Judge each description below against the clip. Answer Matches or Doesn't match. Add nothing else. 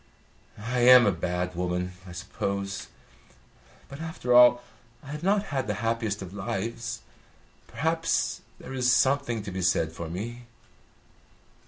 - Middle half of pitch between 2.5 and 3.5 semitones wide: Doesn't match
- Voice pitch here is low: Matches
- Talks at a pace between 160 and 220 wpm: Doesn't match